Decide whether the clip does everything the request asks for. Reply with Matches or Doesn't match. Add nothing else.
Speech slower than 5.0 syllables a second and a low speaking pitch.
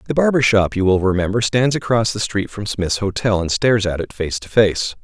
Doesn't match